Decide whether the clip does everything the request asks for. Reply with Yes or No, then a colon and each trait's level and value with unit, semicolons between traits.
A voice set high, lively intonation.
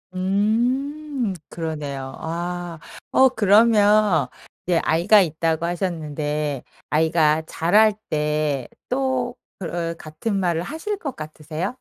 No: medium, 175 Hz; wide, 5.7 semitones